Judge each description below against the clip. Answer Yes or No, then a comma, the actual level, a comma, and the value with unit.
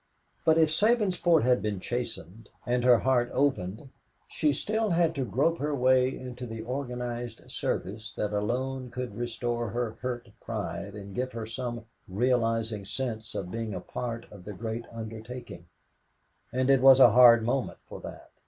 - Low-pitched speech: Yes, low, 120 Hz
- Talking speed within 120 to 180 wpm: Yes, average, 160 wpm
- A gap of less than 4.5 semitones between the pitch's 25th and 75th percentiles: Yes, average, 2.7 semitones